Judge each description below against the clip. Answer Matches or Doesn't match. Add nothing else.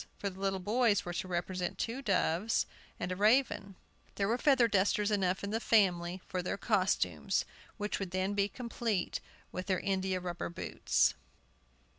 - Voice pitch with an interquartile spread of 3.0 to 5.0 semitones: Doesn't match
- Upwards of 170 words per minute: Doesn't match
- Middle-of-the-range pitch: Doesn't match